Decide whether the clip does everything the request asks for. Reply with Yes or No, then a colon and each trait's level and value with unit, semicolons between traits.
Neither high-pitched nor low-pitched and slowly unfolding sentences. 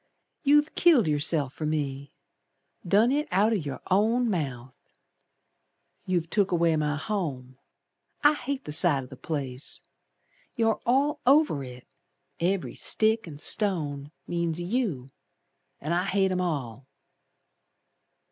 Yes: medium, 170 Hz; slow, 130 wpm